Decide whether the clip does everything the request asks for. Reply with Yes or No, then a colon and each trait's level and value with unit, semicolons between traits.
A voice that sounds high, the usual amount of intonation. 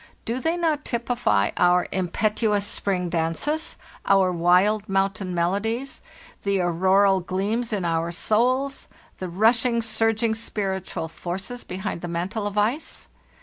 Yes: high, 200 Hz; average, 4.0 semitones